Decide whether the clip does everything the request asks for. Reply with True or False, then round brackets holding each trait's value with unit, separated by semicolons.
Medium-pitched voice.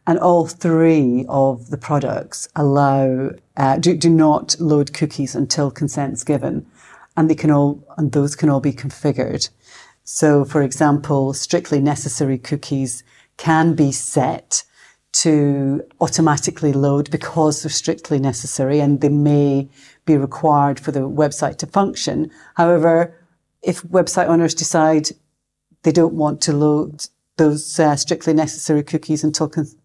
True (150 Hz)